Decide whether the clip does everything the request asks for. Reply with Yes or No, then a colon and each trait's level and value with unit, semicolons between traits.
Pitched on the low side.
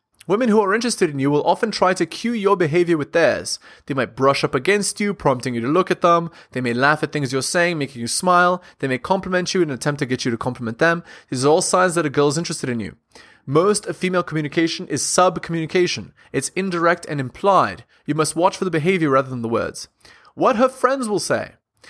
No: medium, 170 Hz